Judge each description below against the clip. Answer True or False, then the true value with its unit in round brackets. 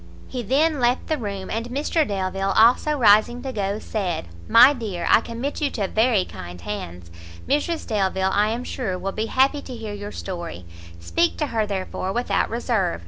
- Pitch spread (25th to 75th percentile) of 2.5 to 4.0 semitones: False (4.8 semitones)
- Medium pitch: False (220 Hz)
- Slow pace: False (185 wpm)